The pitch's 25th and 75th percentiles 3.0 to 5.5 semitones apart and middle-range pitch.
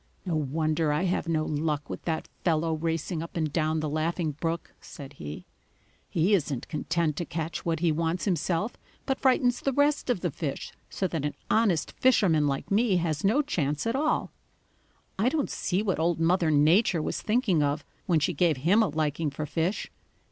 Yes: average, 3.7 semitones; medium, 165 Hz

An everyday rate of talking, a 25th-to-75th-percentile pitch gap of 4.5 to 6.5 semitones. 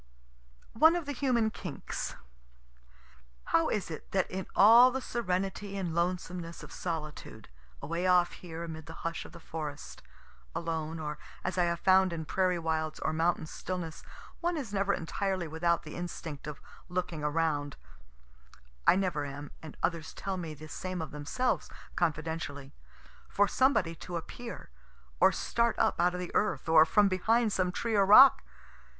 No: average, 160 wpm; average, 3.6 semitones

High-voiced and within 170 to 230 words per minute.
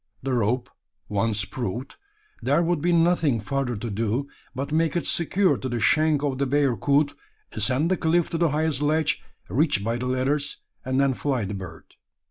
No: medium, 140 Hz; average, 180 wpm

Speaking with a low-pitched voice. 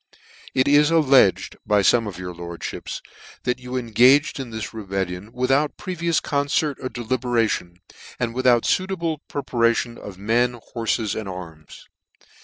Yes: low, 120 Hz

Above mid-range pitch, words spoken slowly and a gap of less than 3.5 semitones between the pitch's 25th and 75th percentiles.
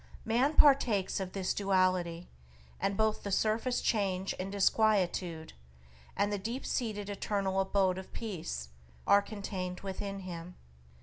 Yes: high, 195 Hz; slow, 130 wpm; narrow, 2.6 semitones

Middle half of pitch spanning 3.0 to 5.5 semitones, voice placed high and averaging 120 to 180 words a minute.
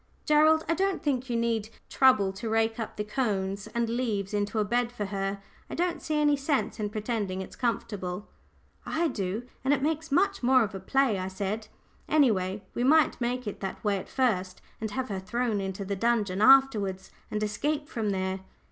No: average, 5.0 semitones; high, 225 Hz; average, 200 wpm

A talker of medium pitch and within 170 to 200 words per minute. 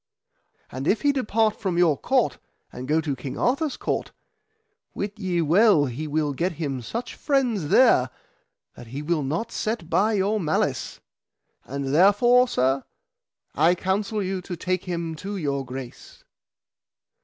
No: medium, 175 Hz; average, 150 wpm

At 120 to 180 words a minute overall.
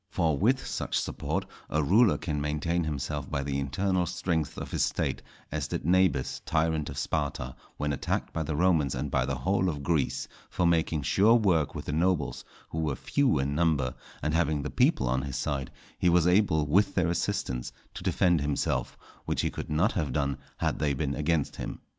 No: average, 195 wpm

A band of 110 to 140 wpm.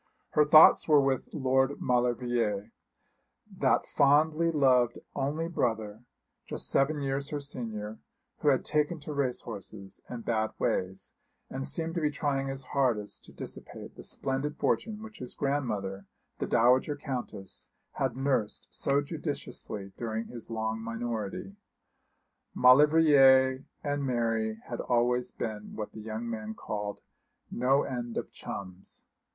Yes: slow, 135 wpm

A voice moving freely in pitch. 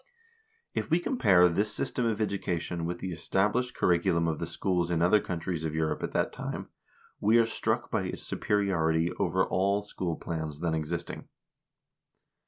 No: average, 3.6 semitones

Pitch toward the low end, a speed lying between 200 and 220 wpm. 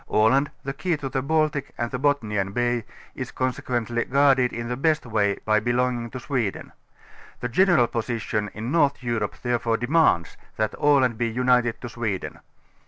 No: low, 120 Hz; average, 170 wpm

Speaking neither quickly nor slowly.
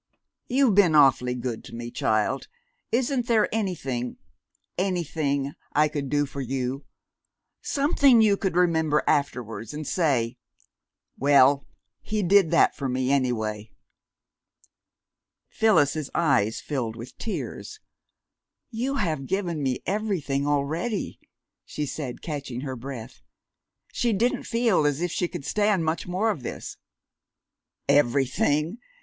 No: slow, 125 wpm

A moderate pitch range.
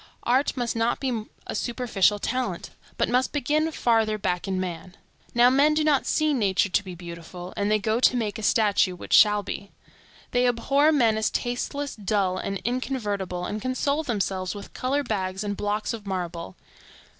Yes: average, 4.6 semitones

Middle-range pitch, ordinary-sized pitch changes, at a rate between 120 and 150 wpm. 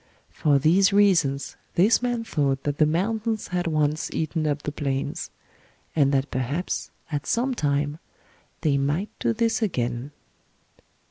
No: medium, 155 Hz; wide, 5.8 semitones; average, 140 wpm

